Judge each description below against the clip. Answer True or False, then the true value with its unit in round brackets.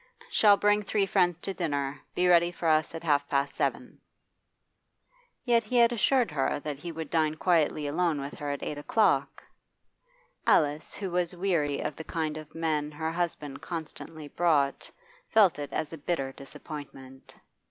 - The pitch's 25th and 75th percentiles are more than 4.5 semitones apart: False (3.4 semitones)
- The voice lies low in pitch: False (160 Hz)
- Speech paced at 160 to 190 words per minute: True (165 wpm)